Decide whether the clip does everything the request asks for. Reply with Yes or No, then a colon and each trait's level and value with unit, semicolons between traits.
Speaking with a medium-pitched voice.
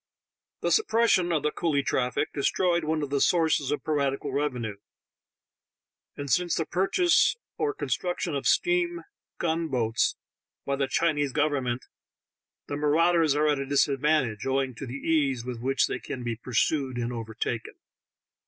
Yes: medium, 145 Hz